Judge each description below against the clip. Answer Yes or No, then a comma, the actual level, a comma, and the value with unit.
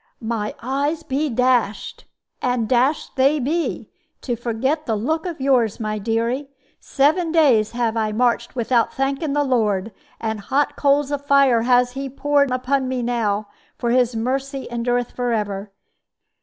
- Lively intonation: No, average, 3.4 semitones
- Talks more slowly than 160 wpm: Yes, average, 150 wpm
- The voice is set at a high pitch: Yes, very high, 250 Hz